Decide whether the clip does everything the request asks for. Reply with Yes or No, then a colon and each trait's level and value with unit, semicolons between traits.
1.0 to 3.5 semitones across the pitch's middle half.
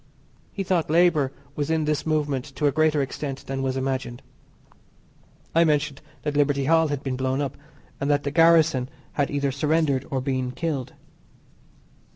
Yes: narrow, 2.6 semitones